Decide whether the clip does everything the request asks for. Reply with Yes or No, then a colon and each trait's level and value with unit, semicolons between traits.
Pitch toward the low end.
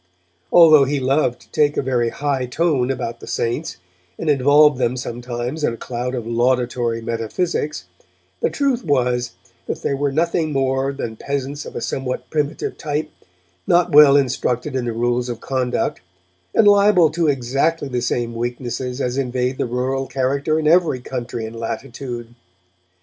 Yes: low, 130 Hz